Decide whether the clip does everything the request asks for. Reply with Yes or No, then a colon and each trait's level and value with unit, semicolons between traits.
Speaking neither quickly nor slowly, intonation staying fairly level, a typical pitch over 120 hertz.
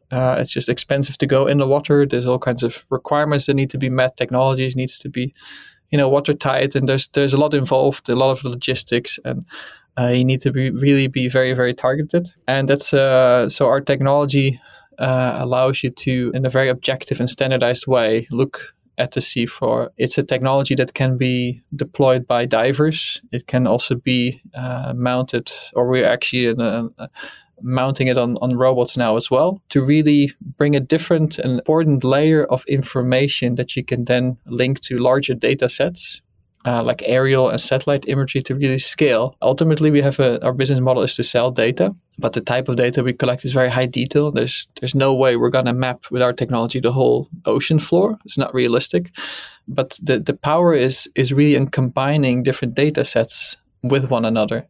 No: fast, 200 wpm; narrow, 1.8 semitones; low, 130 Hz